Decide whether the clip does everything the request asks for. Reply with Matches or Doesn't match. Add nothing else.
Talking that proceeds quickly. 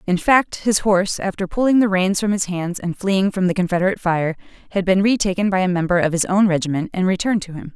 Matches